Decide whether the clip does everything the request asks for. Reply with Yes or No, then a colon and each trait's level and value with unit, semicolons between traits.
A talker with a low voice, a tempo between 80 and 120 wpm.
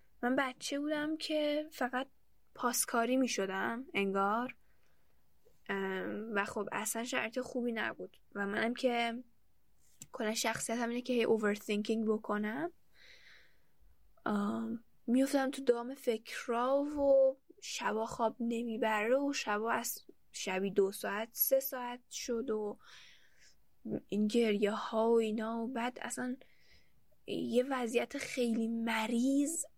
No: high, 235 Hz; average, 110 wpm